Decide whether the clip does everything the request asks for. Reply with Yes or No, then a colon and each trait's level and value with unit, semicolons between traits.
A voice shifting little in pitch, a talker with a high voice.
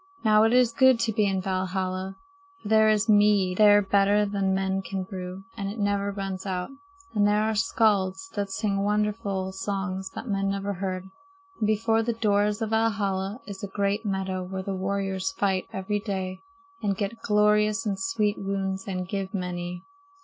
Yes: narrow, 1.8 semitones; high, 200 Hz